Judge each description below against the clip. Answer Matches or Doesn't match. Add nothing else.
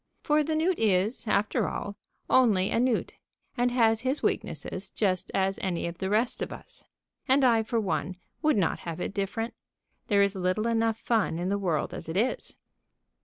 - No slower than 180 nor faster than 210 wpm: Matches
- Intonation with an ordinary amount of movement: Matches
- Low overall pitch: Doesn't match